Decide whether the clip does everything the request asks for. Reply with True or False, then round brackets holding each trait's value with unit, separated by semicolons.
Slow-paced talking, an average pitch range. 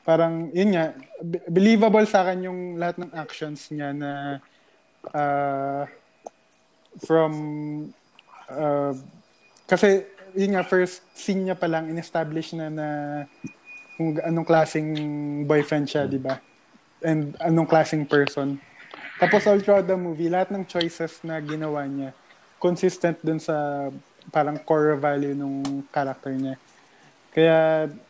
True (120 wpm; 3.0 semitones)